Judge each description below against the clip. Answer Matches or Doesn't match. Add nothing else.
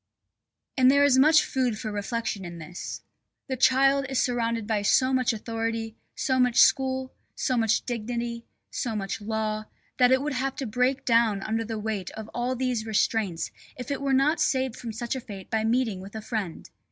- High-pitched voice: Matches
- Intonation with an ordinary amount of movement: Matches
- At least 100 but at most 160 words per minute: Doesn't match